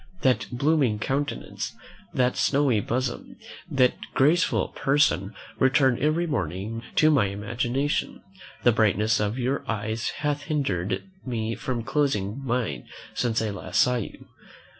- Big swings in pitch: No, average, 4.5 semitones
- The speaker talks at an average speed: No, slow, 125 wpm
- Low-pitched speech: Yes, low, 120 Hz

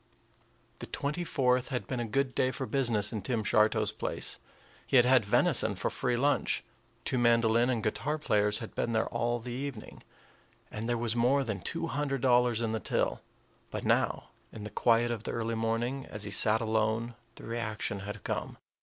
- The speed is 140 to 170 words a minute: No, average, 190 wpm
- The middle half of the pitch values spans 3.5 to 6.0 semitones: No, narrow, 2.6 semitones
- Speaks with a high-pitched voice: No, low, 120 Hz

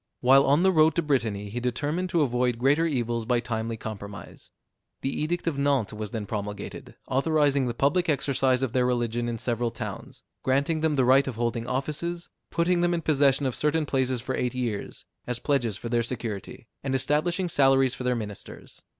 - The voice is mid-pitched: No, low, 130 Hz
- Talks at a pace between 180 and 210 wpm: Yes, average, 190 wpm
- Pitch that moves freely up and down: No, average, 3.9 semitones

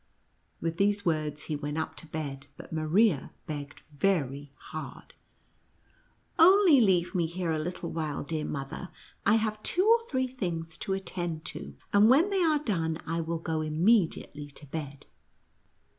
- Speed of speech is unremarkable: Yes, average, 160 wpm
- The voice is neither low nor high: Yes, medium, 165 Hz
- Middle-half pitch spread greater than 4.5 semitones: Yes, average, 5.3 semitones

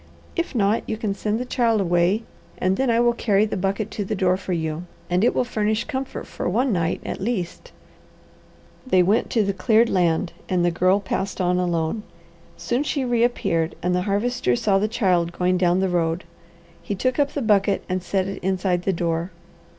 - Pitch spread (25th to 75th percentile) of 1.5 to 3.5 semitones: No, average, 3.9 semitones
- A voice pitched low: No, high, 195 Hz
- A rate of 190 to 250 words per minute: Yes, average, 200 wpm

